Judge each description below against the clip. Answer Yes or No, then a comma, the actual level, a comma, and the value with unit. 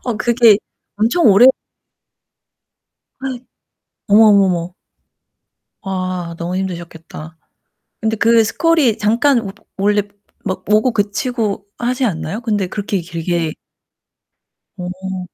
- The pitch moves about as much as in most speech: Yes, average, 4.0 semitones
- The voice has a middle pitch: No, high, 205 Hz